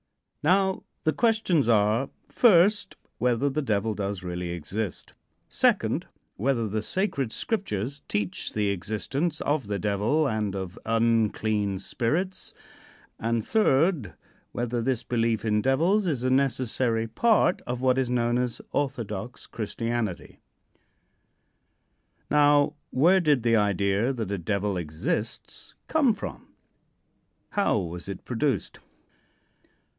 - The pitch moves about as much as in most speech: No, wide, 5.7 semitones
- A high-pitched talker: No, low, 115 Hz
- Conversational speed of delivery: No, slow, 120 wpm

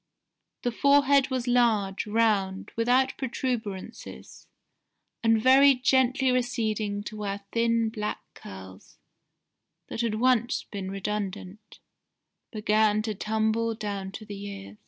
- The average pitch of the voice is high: Yes, high, 220 Hz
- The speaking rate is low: Yes, slow, 115 wpm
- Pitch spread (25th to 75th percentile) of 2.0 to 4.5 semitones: Yes, average, 3.2 semitones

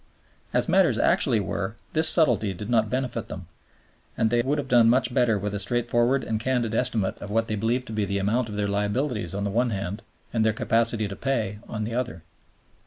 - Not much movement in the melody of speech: No, average, 3.0 semitones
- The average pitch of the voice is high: No, low, 115 Hz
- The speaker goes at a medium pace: No, fast, 215 wpm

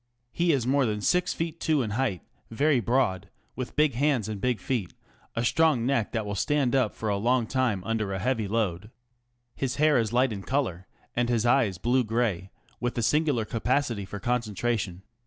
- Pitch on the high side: No, low, 120 Hz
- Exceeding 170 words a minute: Yes, average, 195 wpm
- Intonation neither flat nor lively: Yes, average, 4.2 semitones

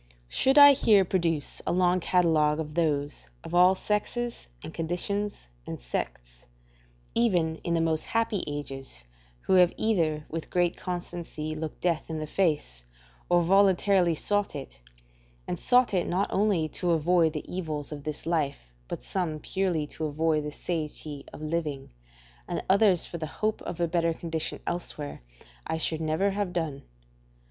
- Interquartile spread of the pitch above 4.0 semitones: No, average, 3.4 semitones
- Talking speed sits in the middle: Yes, average, 160 wpm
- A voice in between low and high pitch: Yes, medium, 165 Hz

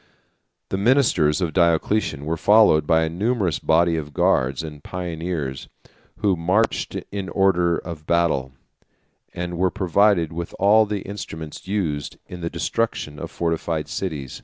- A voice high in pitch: No, very low, 85 Hz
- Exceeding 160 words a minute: No, average, 140 wpm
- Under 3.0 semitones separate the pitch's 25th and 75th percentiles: No, average, 3.6 semitones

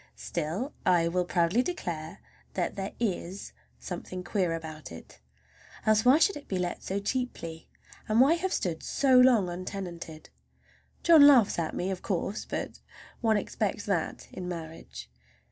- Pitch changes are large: Yes, wide, 5.7 semitones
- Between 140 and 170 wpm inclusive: Yes, average, 150 wpm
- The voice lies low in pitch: No, high, 190 Hz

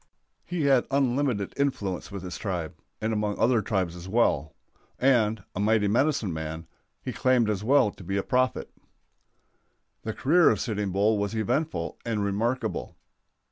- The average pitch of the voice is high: No, low, 110 Hz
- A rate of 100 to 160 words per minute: Yes, average, 155 wpm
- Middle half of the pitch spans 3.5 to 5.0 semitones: Yes, average, 4.5 semitones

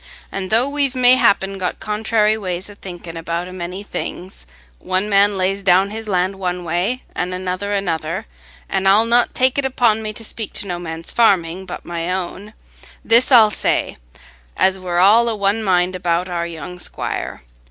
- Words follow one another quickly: No, average, 170 wpm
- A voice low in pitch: No, high, 190 Hz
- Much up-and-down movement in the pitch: No, average, 3.3 semitones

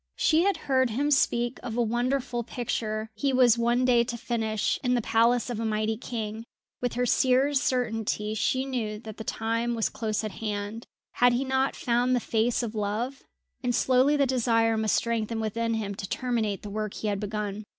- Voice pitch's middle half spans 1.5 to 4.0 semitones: Yes, narrow, 2.4 semitones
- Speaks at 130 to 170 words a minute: No, average, 195 wpm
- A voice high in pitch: Yes, high, 235 Hz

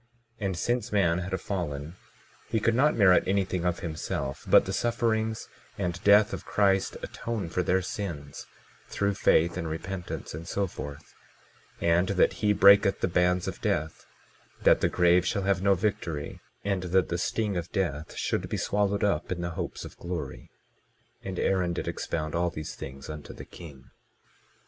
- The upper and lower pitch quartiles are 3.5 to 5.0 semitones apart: No, average, 3.0 semitones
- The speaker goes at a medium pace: Yes, average, 175 wpm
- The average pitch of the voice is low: Yes, very low, 90 Hz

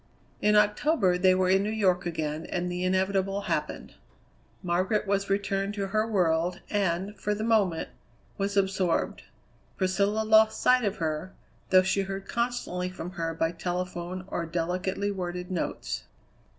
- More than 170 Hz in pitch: Yes, high, 190 Hz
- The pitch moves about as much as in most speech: No, narrow, 2.3 semitones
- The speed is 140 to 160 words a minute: Yes, average, 150 wpm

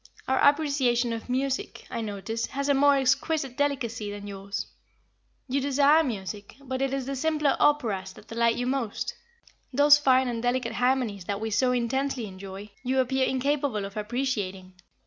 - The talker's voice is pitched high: Yes, very high, 250 Hz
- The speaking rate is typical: Yes, average, 165 wpm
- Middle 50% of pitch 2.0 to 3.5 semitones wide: No, average, 4.3 semitones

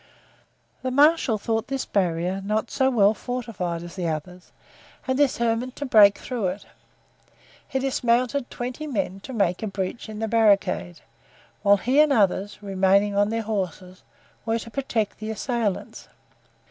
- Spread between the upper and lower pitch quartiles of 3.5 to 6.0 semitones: Yes, average, 4.1 semitones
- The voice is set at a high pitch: Yes, high, 215 Hz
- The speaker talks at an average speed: Yes, average, 150 wpm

